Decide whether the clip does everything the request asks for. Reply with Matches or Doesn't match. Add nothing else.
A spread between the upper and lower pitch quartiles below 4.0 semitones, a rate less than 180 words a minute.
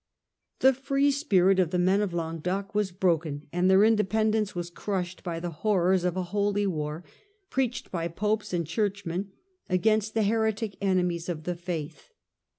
Matches